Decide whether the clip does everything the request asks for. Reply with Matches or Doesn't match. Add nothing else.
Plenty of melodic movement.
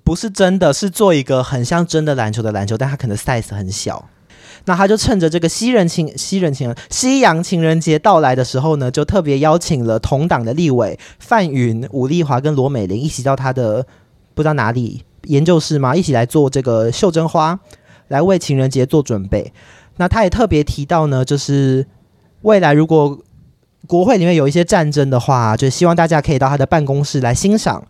Doesn't match